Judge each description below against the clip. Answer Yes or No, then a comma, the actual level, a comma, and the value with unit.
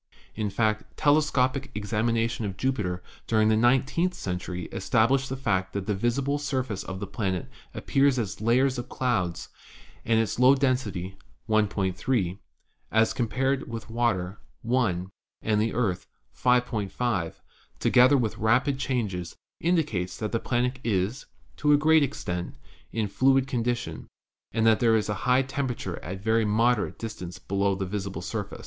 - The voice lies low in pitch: Yes, low, 115 Hz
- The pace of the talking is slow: No, average, 155 wpm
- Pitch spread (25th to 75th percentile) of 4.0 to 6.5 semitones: Yes, average, 4.7 semitones